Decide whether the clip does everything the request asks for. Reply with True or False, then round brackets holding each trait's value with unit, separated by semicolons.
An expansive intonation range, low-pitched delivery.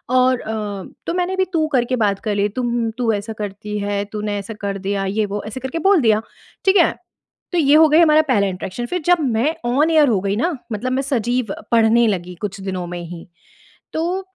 False (6.9 semitones; 230 Hz)